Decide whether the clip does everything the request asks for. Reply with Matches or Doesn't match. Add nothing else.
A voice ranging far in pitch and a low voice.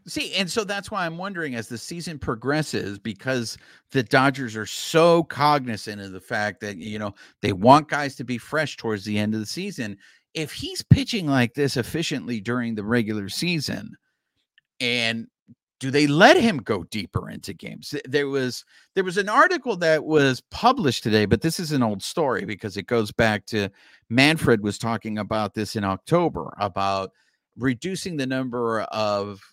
Matches